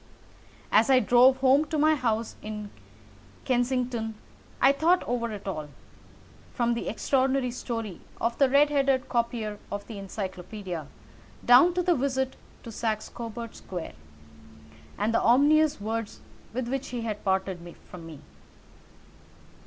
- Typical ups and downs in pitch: Yes, average, 3.9 semitones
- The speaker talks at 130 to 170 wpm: Yes, slow, 135 wpm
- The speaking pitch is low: No, high, 235 Hz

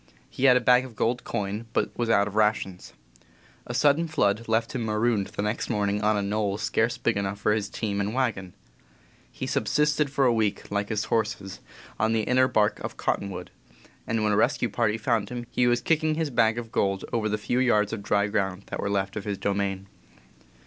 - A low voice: Yes, low, 110 Hz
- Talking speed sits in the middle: No, fast, 215 wpm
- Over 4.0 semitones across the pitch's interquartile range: No, average, 2.9 semitones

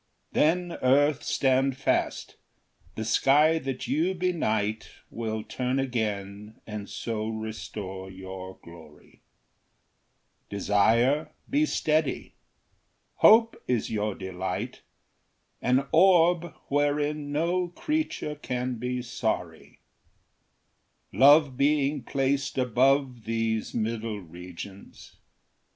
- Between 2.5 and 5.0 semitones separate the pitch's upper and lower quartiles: No, wide, 5.5 semitones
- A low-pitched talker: Yes, low, 125 Hz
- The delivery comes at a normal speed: No, slow, 90 wpm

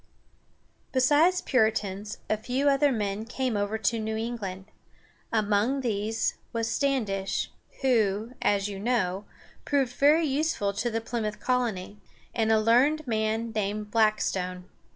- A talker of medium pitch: No, high, 220 Hz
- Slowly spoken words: Yes, slow, 130 wpm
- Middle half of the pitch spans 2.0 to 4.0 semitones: Yes, average, 3.6 semitones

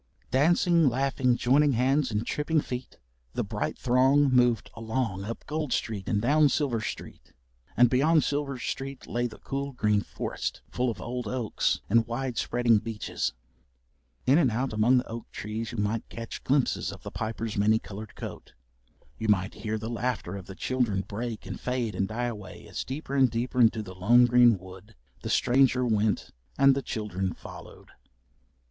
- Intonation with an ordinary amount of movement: Yes, average, 3.4 semitones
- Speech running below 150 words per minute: No, average, 175 wpm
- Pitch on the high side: No, low, 120 Hz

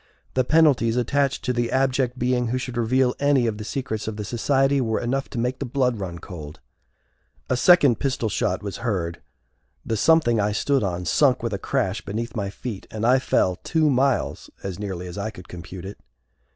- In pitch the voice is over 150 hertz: No, low, 120 Hz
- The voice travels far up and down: No, average, 4.4 semitones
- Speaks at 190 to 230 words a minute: Yes, average, 200 wpm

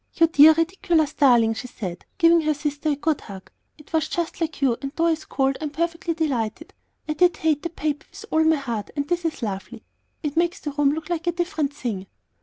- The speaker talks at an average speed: No, fast, 225 wpm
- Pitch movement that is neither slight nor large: Yes, average, 3.2 semitones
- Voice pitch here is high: Yes, very high, 305 Hz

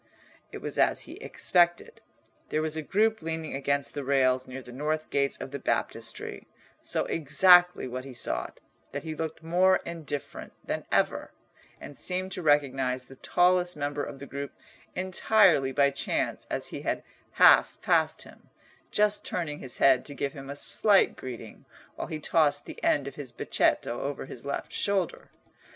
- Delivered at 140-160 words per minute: No, average, 170 wpm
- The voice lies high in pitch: No, medium, 145 Hz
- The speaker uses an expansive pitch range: No, average, 4.2 semitones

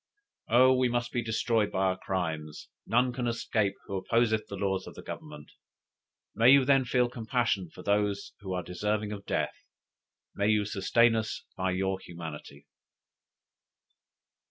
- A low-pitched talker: Yes, low, 105 Hz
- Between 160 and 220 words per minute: No, average, 150 wpm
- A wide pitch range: No, average, 4.0 semitones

